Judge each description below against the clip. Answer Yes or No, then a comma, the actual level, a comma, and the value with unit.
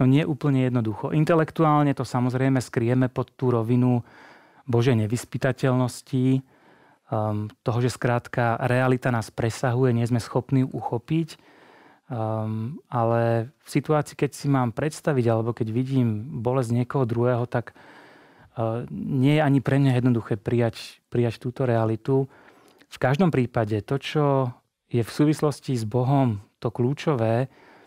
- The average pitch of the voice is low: Yes, low, 125 Hz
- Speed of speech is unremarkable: Yes, average, 140 wpm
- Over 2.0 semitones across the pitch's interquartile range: Yes, narrow, 2.6 semitones